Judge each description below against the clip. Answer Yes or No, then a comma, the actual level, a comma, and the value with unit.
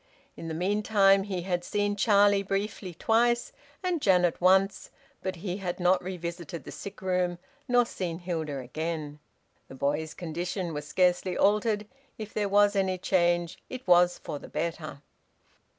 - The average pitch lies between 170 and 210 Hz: Yes, medium, 185 Hz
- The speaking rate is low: No, average, 150 wpm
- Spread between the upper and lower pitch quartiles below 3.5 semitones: Yes, average, 3.0 semitones